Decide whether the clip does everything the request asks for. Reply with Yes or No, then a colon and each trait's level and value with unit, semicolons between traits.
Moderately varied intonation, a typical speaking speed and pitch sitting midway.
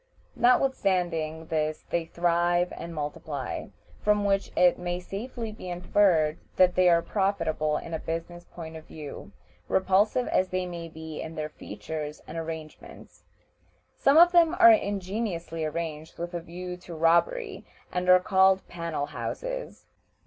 Yes: average, 3.4 semitones; average, 145 wpm; medium, 175 Hz